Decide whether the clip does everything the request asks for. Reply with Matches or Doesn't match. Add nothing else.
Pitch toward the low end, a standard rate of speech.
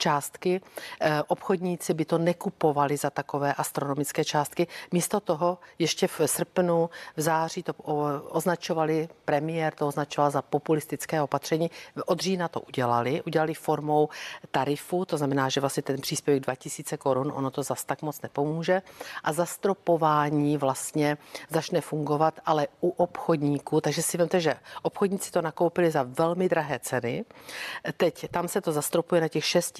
Doesn't match